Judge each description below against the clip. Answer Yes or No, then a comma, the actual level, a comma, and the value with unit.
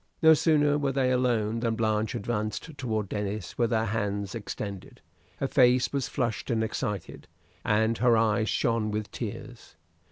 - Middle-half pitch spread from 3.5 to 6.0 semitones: No, average, 2.9 semitones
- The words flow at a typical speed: Yes, average, 155 wpm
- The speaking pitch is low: Yes, low, 115 Hz